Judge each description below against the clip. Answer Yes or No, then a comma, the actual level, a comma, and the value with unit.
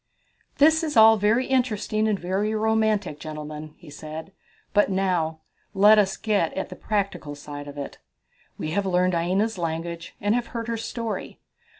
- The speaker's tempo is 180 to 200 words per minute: No, average, 165 wpm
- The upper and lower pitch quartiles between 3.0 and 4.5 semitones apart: No, average, 5.2 semitones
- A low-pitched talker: No, high, 195 Hz